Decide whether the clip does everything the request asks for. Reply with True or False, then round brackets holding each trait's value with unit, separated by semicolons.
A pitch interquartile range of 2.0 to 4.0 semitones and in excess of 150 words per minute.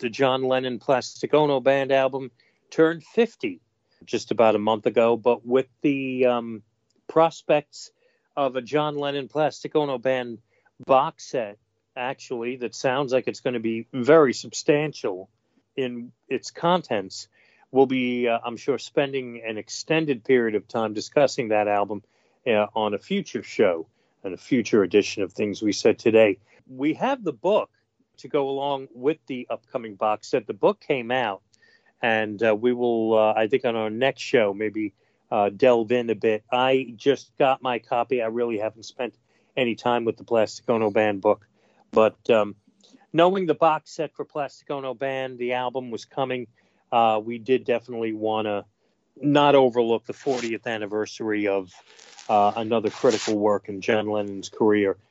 True (3.7 semitones; 165 wpm)